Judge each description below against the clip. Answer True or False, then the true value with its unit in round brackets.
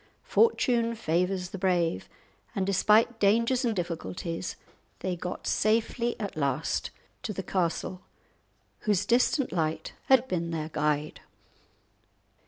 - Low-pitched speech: False (185 Hz)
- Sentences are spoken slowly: True (115 wpm)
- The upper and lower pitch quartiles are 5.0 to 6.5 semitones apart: True (5.5 semitones)